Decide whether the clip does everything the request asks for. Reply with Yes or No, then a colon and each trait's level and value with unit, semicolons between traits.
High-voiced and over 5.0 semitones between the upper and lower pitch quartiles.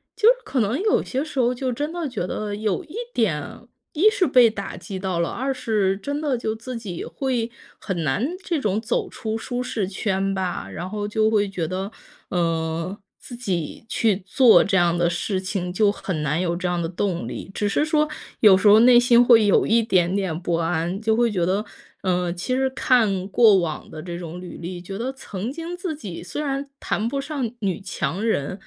Yes: high, 205 Hz; wide, 5.5 semitones